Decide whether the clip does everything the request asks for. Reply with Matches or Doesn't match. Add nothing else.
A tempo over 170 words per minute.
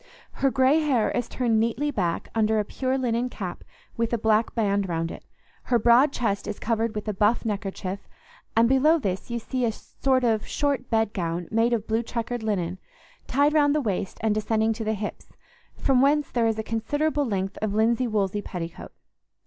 Matches